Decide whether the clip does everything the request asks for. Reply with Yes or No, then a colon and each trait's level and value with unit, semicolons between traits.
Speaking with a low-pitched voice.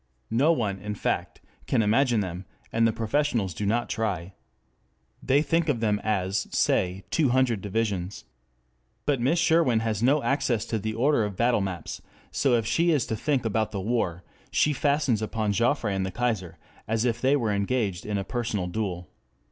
Yes: low, 115 Hz